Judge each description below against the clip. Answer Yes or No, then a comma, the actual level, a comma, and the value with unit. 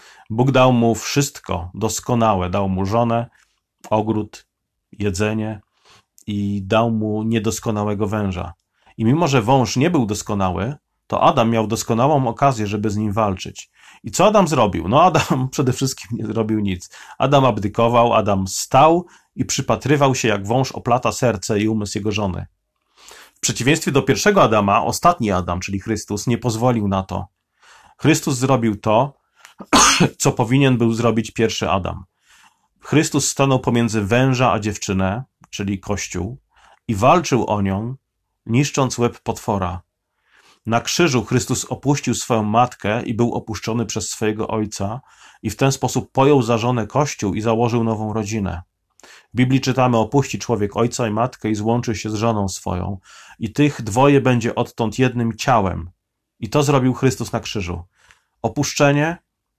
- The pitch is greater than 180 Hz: No, low, 115 Hz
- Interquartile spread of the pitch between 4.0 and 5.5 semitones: No, average, 3.5 semitones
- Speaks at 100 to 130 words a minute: No, average, 145 wpm